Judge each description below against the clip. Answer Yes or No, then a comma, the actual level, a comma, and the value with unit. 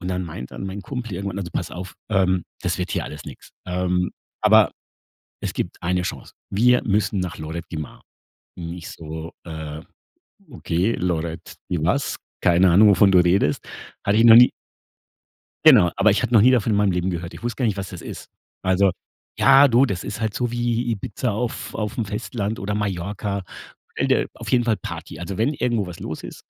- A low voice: Yes, low, 100 Hz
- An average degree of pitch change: Yes, average, 4.2 semitones